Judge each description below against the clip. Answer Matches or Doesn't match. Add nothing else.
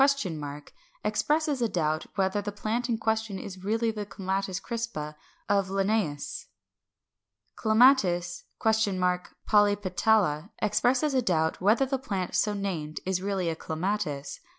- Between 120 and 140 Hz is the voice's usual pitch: Doesn't match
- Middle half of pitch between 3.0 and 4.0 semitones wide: Matches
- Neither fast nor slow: Doesn't match